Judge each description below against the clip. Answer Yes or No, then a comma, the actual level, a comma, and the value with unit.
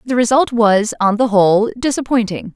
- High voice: Yes, high, 225 Hz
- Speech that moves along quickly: No, average, 165 wpm